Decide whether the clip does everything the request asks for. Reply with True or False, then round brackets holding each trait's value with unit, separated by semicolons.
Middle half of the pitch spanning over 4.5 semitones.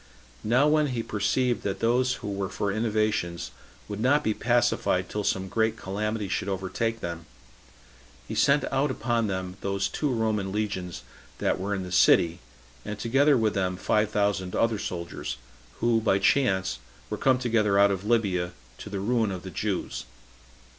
False (3.4 semitones)